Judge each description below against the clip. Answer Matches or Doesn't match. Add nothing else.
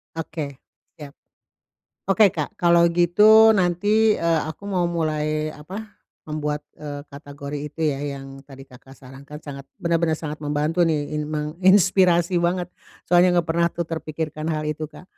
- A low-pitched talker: Doesn't match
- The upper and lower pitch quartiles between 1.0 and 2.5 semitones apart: Doesn't match